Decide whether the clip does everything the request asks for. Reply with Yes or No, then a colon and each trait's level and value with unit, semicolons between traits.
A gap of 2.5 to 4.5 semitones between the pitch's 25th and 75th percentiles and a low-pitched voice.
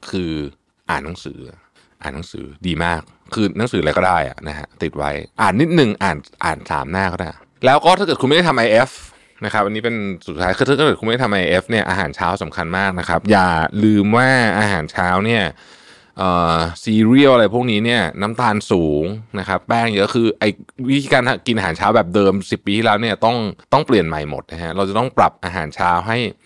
Yes: average, 4.1 semitones; low, 100 Hz